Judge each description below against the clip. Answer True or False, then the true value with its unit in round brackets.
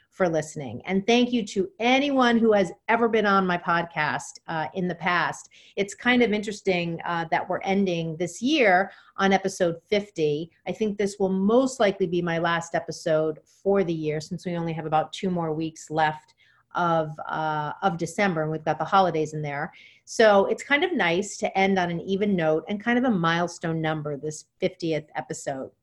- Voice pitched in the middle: True (175 Hz)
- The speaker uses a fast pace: False (195 wpm)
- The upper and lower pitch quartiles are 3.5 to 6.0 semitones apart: True (3.9 semitones)